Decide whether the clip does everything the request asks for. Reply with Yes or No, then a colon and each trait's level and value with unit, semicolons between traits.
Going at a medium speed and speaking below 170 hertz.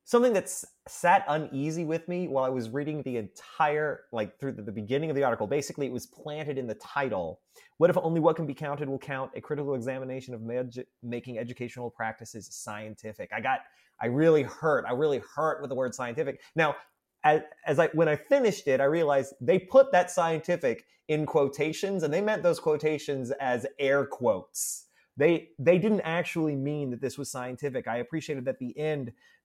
Yes: average, 195 wpm; medium, 140 Hz